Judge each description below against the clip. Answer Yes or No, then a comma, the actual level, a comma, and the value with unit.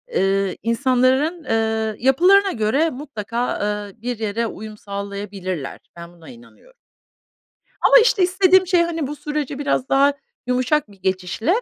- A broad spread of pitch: Yes, wide, 6.6 semitones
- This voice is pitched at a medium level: No, high, 245 Hz